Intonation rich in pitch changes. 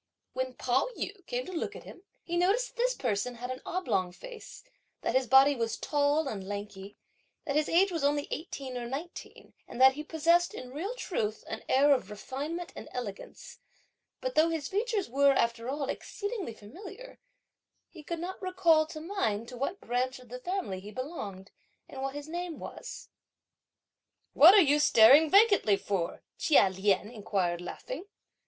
Yes: wide, 6.8 semitones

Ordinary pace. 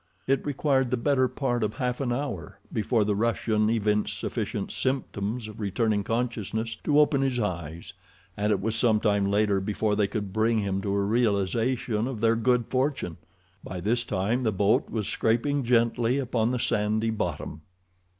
Yes: average, 170 wpm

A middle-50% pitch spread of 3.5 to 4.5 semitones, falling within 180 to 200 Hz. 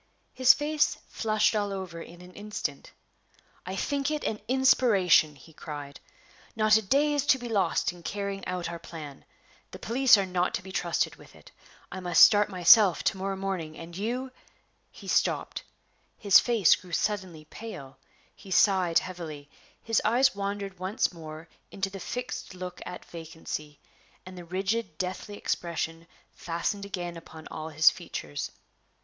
Yes: average, 4.1 semitones; medium, 185 Hz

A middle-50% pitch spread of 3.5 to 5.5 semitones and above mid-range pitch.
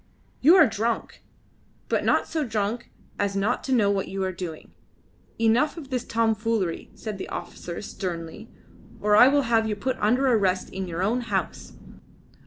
Yes: average, 3.9 semitones; high, 220 Hz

